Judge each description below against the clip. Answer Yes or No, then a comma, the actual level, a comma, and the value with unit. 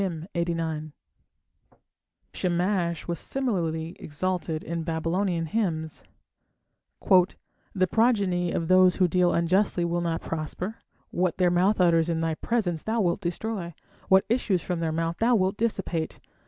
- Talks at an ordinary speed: No, slow, 125 wpm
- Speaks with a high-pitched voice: No, medium, 175 Hz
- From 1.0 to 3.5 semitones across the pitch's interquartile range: Yes, narrow, 2.6 semitones